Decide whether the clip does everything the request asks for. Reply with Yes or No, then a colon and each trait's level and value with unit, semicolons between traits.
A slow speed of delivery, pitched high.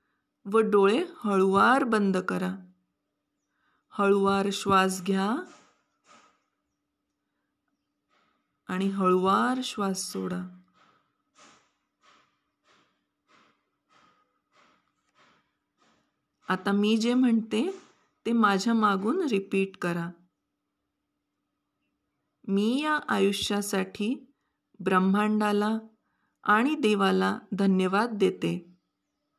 Yes: slow, 60 wpm; high, 200 Hz